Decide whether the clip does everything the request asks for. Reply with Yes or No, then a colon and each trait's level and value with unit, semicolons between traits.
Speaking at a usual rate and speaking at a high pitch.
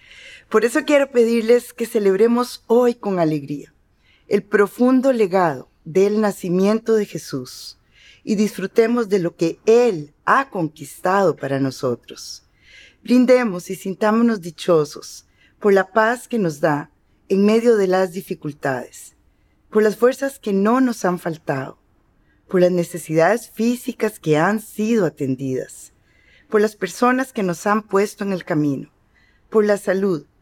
Yes: average, 140 wpm; high, 200 Hz